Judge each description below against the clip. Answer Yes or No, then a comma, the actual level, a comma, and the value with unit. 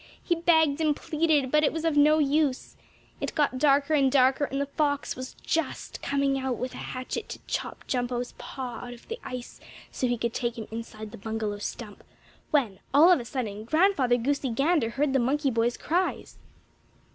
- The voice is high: Yes, very high, 270 Hz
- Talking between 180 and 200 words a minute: Yes, average, 190 wpm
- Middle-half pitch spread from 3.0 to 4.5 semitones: Yes, average, 3.8 semitones